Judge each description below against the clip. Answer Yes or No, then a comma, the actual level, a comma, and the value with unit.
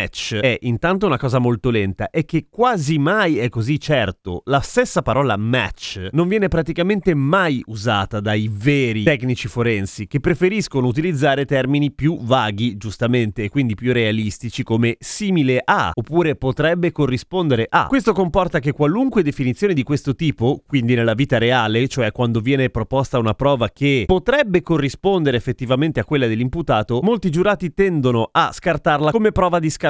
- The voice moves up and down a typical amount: No, wide, 5.7 semitones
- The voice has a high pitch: No, low, 135 Hz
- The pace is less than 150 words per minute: No, average, 155 wpm